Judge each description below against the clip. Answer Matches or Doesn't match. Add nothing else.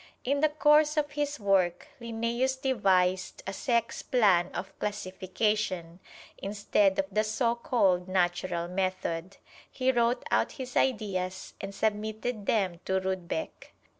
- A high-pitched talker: Matches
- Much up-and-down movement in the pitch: Doesn't match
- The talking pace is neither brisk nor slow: Doesn't match